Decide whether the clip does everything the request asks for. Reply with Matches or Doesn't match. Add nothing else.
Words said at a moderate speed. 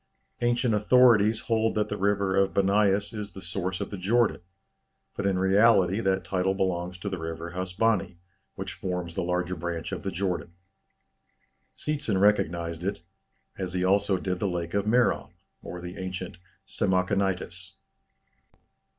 Matches